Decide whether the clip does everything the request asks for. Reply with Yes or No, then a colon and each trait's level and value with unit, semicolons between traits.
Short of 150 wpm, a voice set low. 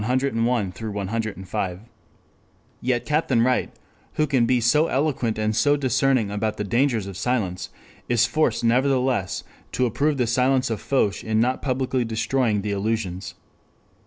Yes: slow, 135 wpm; low, 120 Hz